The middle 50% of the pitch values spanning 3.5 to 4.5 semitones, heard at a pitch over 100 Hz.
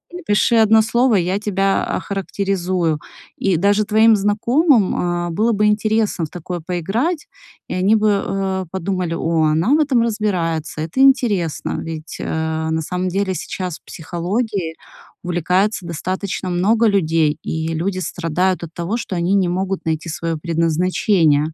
Yes: average, 4.0 semitones; medium, 185 Hz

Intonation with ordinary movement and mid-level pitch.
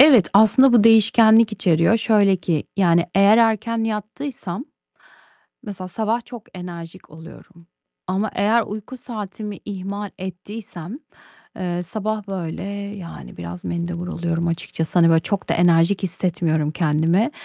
No: average, 4.3 semitones; high, 195 Hz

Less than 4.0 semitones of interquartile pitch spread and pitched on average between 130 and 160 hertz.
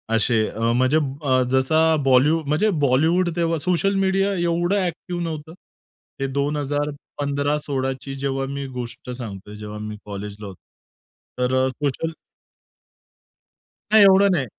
No: average, 4.4 semitones; medium, 140 Hz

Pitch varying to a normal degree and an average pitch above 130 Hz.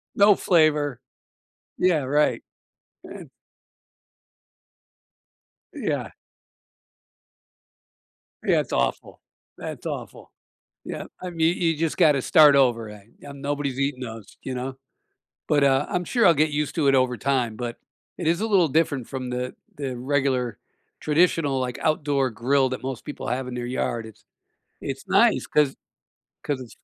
Yes: average, 3.3 semitones; medium, 140 Hz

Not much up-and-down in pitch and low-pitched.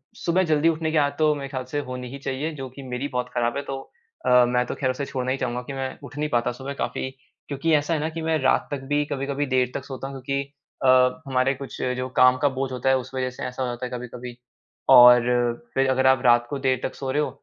Yes: narrow, 2.1 semitones; low, 130 Hz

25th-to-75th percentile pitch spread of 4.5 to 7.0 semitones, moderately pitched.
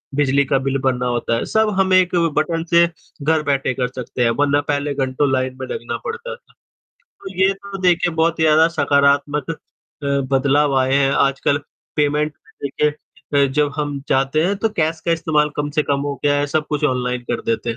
No: average, 3.1 semitones; medium, 145 Hz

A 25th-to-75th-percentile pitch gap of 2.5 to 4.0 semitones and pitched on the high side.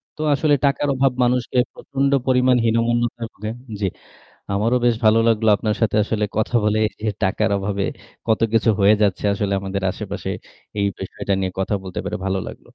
No: average, 3.0 semitones; low, 110 Hz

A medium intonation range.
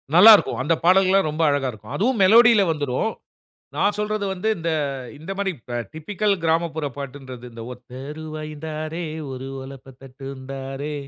No: wide, 6.0 semitones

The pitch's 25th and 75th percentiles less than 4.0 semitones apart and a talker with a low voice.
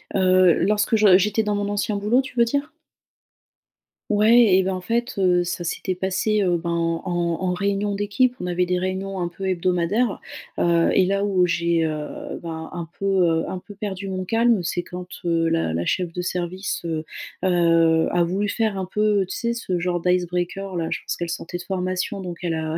No: average, 2.8 semitones; medium, 185 Hz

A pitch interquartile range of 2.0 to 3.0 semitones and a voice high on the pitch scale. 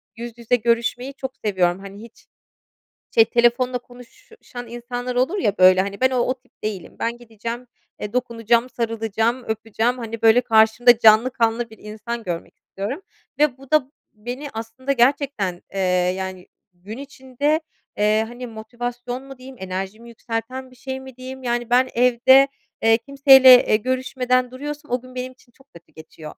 Yes: narrow, 2.6 semitones; high, 240 Hz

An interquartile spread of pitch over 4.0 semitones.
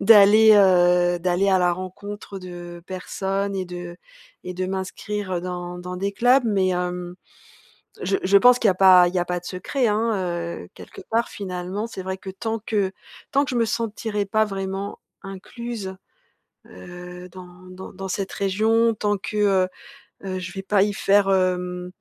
No: narrow, 2.4 semitones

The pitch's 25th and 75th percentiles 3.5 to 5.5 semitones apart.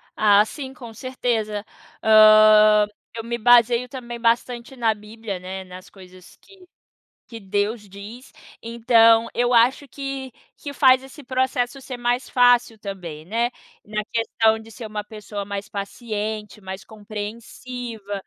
No: average, 2.8 semitones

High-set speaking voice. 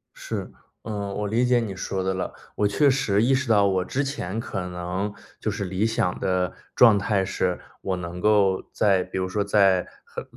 No: low, 100 Hz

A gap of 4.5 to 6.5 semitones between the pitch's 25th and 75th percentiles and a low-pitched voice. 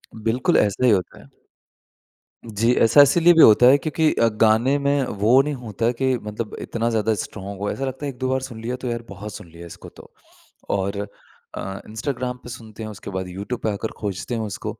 No: average, 3.8 semitones; low, 115 Hz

